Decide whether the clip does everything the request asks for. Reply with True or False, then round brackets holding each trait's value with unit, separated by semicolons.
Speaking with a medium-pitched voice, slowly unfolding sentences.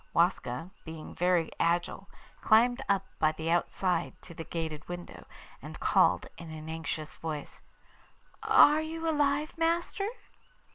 True (175 Hz; 130 wpm)